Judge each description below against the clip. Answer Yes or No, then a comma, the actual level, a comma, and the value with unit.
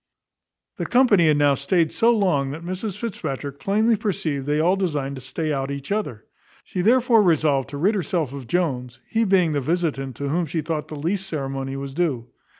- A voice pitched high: No, medium, 155 Hz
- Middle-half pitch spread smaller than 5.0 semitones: No, wide, 5.5 semitones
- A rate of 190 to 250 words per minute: Yes, average, 195 wpm